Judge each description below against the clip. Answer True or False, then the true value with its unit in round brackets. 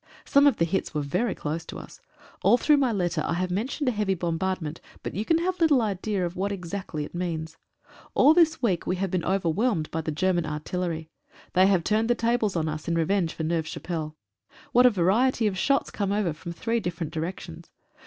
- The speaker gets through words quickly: True (215 wpm)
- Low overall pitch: False (185 Hz)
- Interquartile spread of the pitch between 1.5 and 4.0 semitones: False (5.1 semitones)